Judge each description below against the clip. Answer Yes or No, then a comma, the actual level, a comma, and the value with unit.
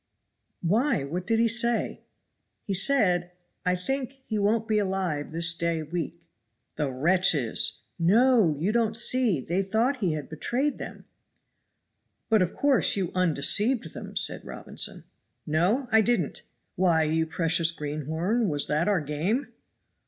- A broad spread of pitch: Yes, wide, 5.9 semitones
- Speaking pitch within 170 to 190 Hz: Yes, medium, 185 Hz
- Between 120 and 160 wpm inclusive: Yes, average, 145 wpm